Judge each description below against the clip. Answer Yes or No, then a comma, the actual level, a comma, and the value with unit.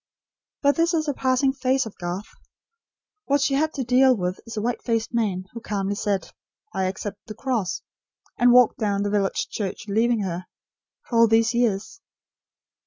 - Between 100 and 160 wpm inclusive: No, average, 175 wpm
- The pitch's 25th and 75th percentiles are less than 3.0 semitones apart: No, average, 4.3 semitones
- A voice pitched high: Yes, high, 230 Hz